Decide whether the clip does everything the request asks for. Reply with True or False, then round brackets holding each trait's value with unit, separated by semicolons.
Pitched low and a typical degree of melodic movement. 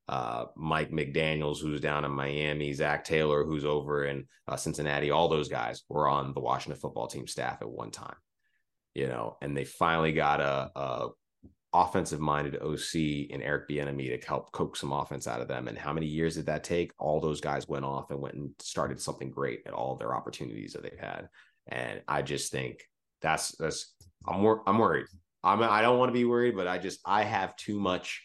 False (75 Hz; 2.1 semitones)